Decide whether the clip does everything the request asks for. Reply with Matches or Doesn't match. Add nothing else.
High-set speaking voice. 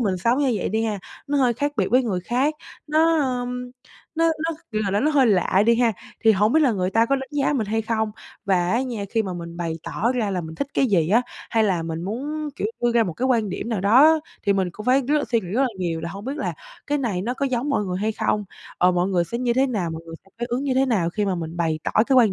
Matches